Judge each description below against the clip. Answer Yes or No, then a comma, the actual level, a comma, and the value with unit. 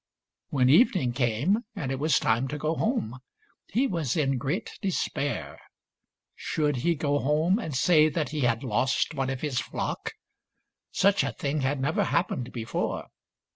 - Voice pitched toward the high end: No, medium, 145 Hz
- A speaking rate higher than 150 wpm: Yes, average, 160 wpm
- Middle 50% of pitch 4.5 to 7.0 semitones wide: No, average, 4.0 semitones